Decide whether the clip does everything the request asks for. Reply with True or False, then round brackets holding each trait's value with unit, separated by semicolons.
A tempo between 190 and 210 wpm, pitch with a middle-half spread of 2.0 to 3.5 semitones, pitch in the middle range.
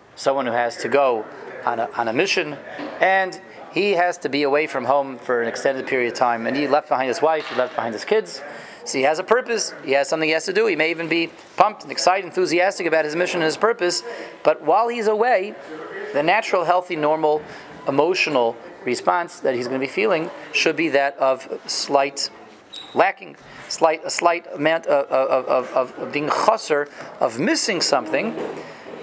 False (200 wpm; 4.5 semitones; 155 Hz)